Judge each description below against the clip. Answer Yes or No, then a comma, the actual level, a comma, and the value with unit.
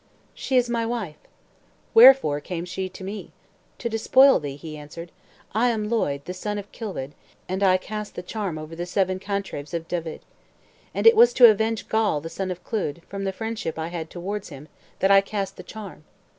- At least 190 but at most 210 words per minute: Yes, average, 200 wpm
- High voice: Yes, high, 195 Hz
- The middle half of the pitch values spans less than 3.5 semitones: No, average, 4.7 semitones